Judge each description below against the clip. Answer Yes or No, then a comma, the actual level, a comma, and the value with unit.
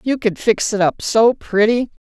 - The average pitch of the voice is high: Yes, high, 220 Hz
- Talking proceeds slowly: No, average, 200 wpm